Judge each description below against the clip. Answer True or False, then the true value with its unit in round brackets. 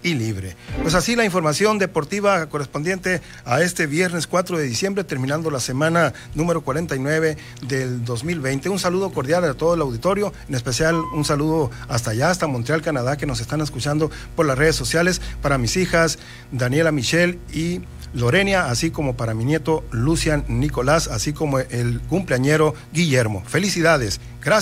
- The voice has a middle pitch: True (155 Hz)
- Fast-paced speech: False (160 wpm)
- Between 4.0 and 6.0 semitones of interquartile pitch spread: True (4.6 semitones)